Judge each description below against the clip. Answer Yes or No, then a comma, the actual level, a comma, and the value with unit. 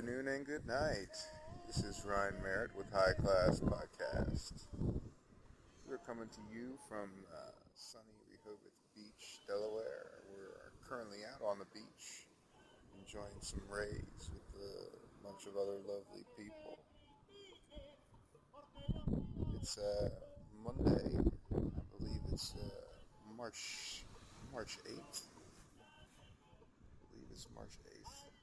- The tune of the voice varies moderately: No, wide, 7.4 semitones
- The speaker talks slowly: Yes, slow, 115 wpm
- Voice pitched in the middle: No, low, 105 Hz